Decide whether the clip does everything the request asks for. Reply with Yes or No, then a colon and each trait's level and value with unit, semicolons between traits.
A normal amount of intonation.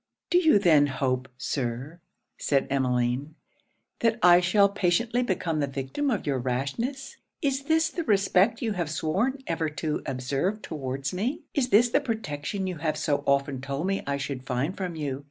No: wide, 7.8 semitones